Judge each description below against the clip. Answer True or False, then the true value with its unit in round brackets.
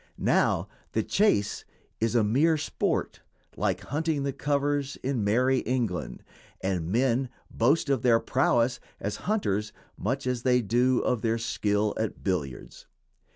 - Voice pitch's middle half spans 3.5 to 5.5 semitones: True (4.3 semitones)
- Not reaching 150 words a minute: True (140 wpm)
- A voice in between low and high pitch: False (125 Hz)